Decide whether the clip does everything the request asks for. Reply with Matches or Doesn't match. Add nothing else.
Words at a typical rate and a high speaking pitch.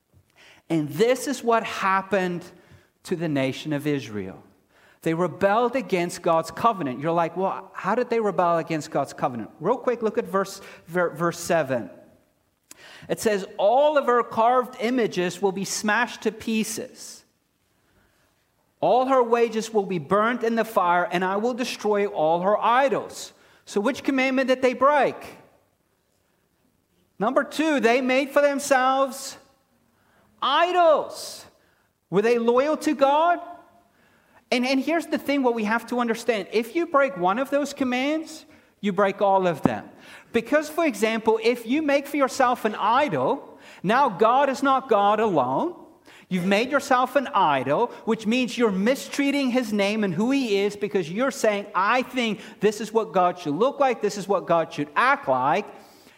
Matches